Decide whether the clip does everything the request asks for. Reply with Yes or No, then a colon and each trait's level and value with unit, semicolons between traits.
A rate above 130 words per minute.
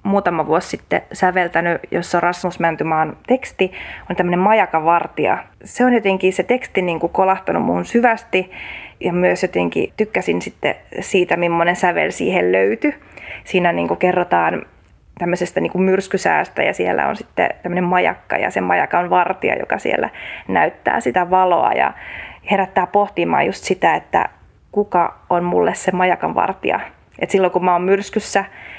Yes: average, 150 wpm